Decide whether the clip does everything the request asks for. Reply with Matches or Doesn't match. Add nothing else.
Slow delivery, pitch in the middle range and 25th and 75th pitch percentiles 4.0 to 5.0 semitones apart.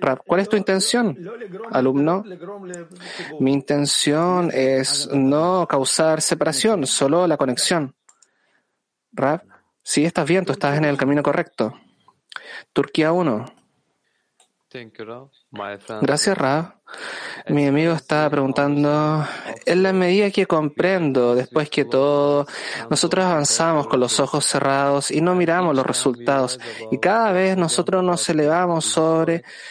Matches